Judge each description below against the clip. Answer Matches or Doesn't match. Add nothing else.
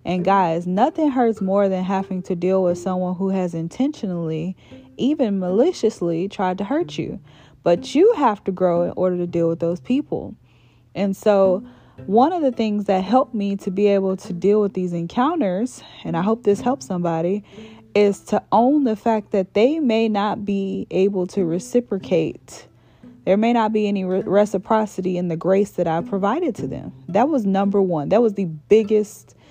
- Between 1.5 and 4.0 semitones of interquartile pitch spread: Matches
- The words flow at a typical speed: Matches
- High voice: Matches